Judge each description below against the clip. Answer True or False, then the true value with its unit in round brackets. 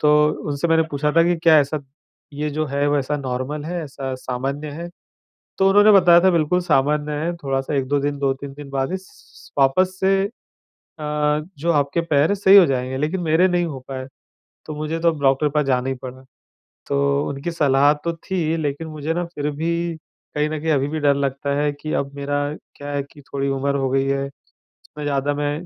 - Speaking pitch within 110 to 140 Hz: False (150 Hz)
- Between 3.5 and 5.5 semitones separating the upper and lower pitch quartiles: False (2.8 semitones)